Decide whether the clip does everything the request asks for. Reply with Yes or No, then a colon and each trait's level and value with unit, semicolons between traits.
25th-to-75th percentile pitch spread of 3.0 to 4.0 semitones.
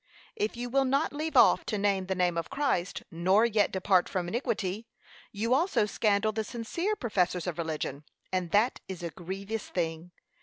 No: average, 4.7 semitones